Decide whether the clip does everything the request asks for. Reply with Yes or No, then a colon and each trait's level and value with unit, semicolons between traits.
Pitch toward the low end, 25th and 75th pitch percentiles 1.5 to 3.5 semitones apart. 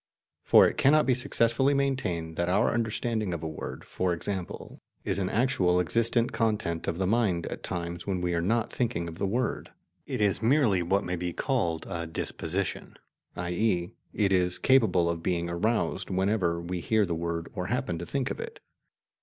No: very low, 95 Hz; average, 5.1 semitones